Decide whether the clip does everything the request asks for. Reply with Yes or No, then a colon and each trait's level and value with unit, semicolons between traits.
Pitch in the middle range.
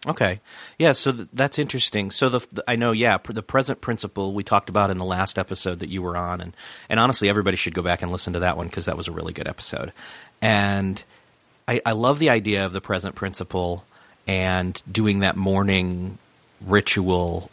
No: low, 100 Hz